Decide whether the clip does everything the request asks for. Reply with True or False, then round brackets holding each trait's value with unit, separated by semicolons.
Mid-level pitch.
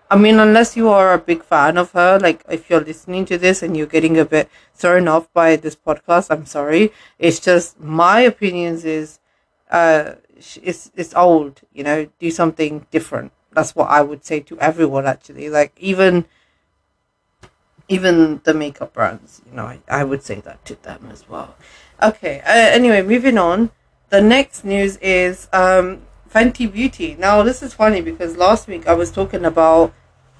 True (170 Hz)